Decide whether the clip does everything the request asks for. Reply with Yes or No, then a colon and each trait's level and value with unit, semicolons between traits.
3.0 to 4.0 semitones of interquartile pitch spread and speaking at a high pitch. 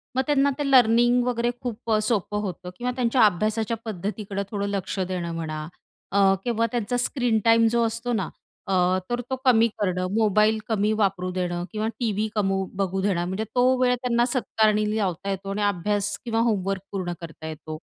Yes: average, 3.5 semitones; high, 210 Hz